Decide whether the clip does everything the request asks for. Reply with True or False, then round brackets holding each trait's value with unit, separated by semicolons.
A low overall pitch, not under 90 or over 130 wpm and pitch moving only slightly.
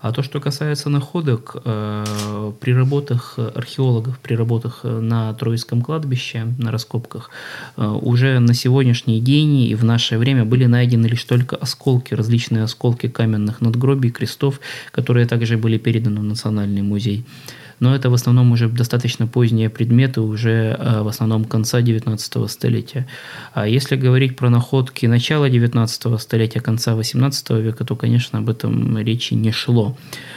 False (120 Hz; 145 wpm; 2.3 semitones)